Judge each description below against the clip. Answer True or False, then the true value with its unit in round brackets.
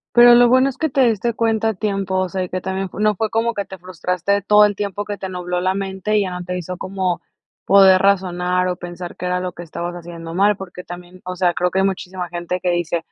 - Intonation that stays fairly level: True (2.3 semitones)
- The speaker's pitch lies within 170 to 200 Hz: True (185 Hz)